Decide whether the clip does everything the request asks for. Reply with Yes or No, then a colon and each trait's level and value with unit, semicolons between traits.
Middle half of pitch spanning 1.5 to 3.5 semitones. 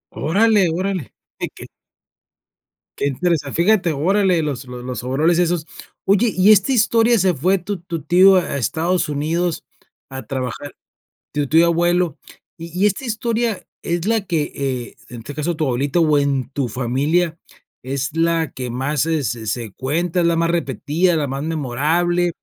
No: average, 4.3 semitones